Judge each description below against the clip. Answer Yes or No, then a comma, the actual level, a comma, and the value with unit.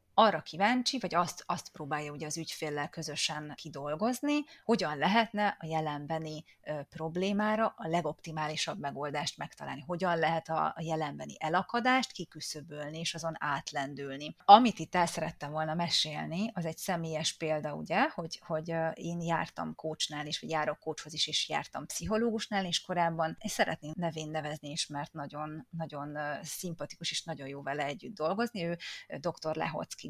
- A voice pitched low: No, medium, 160 Hz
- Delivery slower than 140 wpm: No, average, 150 wpm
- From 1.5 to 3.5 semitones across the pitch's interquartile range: Yes, average, 2.8 semitones